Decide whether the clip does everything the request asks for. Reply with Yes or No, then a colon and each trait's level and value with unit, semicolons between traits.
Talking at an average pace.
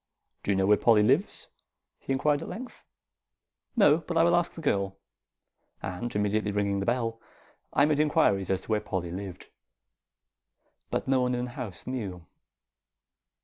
Yes: average, 165 wpm